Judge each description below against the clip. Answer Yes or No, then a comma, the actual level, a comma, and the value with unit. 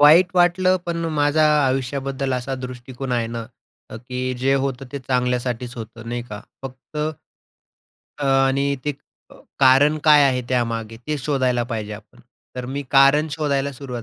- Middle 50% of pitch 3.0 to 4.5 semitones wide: No, narrow, 2.5 semitones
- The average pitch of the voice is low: Yes, low, 130 Hz